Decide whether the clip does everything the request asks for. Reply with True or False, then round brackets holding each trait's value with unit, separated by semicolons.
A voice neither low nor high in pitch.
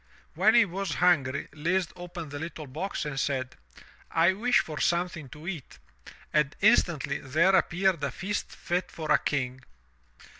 True (170 Hz)